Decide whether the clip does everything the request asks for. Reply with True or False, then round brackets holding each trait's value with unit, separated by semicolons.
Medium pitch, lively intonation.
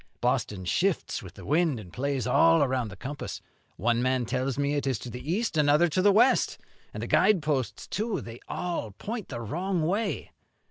True (145 Hz; 6.0 semitones)